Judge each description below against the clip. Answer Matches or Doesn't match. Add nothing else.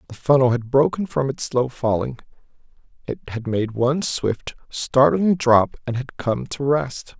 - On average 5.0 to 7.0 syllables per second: Doesn't match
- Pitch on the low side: Matches